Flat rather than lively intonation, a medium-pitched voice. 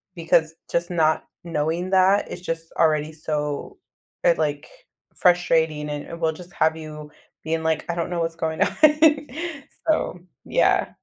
Yes: narrow, 1.9 semitones; medium, 160 Hz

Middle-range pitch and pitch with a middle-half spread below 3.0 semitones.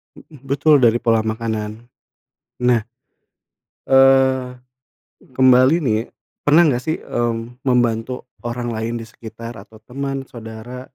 No: low, 120 Hz; narrow, 2.6 semitones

